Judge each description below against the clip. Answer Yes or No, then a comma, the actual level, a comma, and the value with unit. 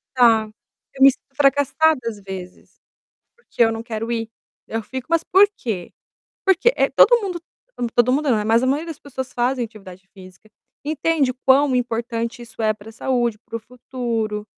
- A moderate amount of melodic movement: Yes, average, 3.7 semitones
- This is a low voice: No, high, 240 Hz